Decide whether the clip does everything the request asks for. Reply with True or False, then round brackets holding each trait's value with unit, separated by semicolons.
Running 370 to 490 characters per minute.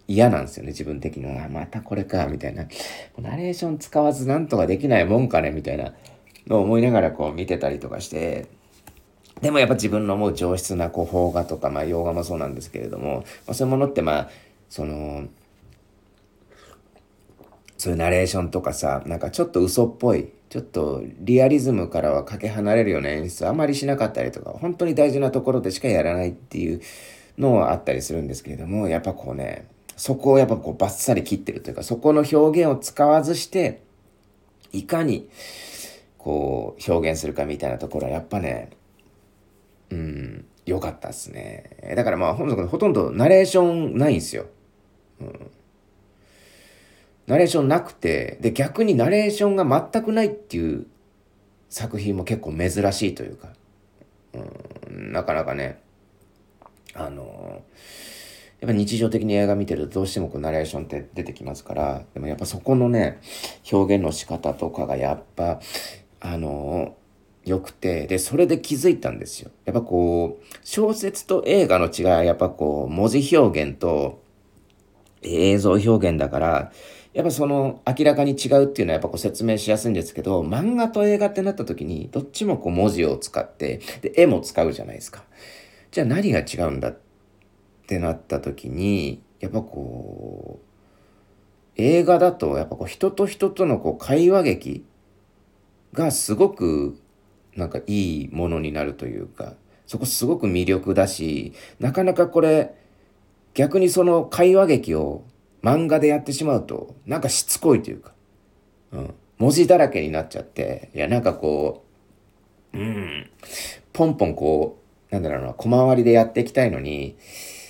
False (335 characters per minute)